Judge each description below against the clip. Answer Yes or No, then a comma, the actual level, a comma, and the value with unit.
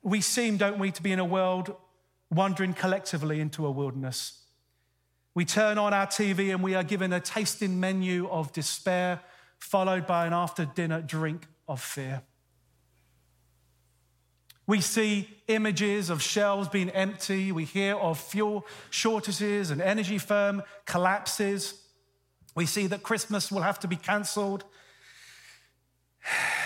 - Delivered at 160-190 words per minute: No, slow, 135 wpm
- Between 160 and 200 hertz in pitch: Yes, medium, 185 Hz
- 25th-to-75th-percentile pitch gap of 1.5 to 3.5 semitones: No, average, 4.3 semitones